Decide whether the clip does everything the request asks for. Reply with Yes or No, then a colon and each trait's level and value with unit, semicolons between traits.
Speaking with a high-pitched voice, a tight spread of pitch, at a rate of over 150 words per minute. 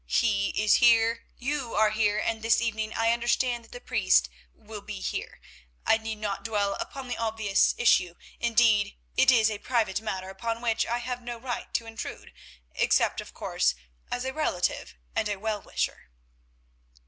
Yes: high, 225 Hz; narrow, 2.3 semitones; average, 170 wpm